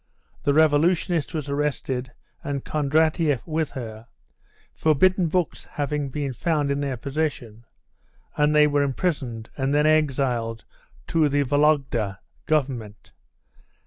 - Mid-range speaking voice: Yes, medium, 145 Hz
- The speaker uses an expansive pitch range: No, average, 2.9 semitones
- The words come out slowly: Yes, slow, 115 wpm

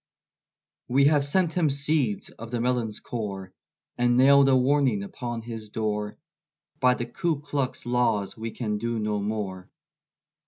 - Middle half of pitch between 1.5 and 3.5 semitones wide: No, average, 4.4 semitones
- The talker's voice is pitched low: Yes, low, 120 Hz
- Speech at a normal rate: Yes, average, 150 wpm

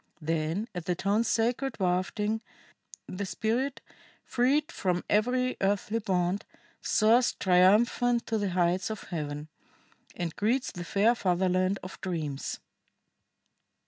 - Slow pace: Yes, slow, 115 wpm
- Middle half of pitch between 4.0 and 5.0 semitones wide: Yes, average, 4.3 semitones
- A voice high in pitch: Yes, high, 200 Hz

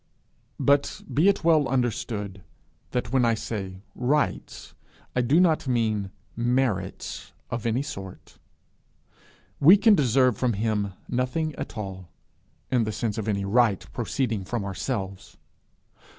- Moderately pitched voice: No, low, 115 Hz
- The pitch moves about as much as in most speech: Yes, average, 4.7 semitones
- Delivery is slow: Yes, slow, 130 wpm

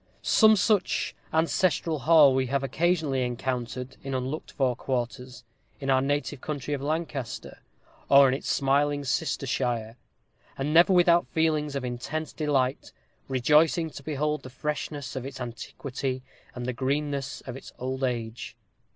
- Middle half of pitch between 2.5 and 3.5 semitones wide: Yes, average, 2.9 semitones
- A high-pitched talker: No, low, 135 Hz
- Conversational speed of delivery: Yes, average, 145 wpm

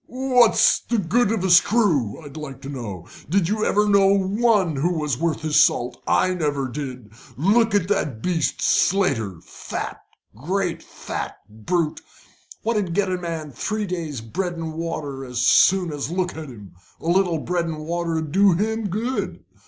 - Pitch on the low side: No, medium, 170 Hz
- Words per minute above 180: No, average, 165 wpm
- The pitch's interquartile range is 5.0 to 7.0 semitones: Yes, average, 5.3 semitones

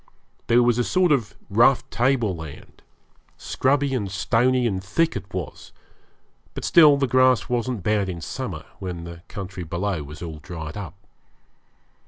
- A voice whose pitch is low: Yes, low, 105 Hz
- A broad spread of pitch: Yes, wide, 6.2 semitones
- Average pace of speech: Yes, average, 155 wpm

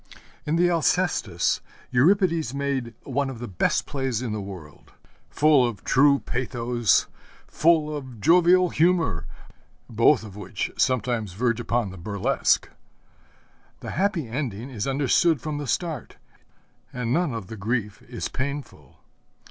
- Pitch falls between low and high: No, low, 125 Hz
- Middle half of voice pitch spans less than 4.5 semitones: No, wide, 5.4 semitones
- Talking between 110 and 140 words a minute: Yes, slow, 135 wpm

